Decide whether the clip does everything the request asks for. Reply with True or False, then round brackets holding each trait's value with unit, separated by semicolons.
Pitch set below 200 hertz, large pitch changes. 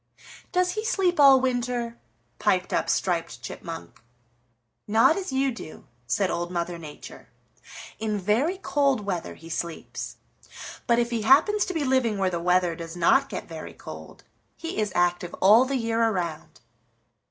False (220 Hz; 7.2 semitones)